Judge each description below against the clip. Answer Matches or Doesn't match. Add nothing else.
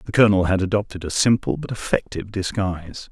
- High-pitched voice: Doesn't match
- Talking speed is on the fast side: Doesn't match